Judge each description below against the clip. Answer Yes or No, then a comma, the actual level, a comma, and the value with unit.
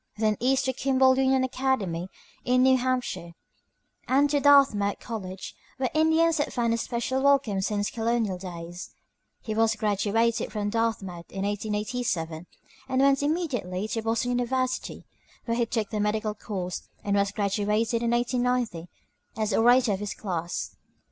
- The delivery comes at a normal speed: Yes, average, 150 wpm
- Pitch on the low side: No, high, 225 Hz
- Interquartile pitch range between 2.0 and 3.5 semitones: No, average, 4.2 semitones